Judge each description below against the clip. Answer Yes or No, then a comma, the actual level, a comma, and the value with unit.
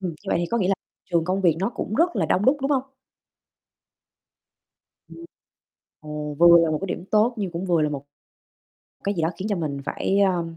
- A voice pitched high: No, medium, 180 Hz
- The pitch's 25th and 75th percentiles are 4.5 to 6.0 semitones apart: No, average, 3.8 semitones